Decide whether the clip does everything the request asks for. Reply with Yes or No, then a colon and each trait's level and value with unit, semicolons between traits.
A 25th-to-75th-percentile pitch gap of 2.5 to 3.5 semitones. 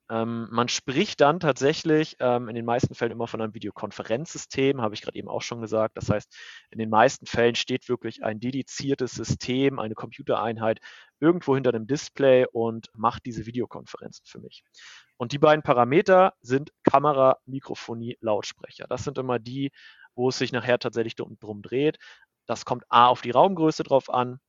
Yes: average, 3.1 semitones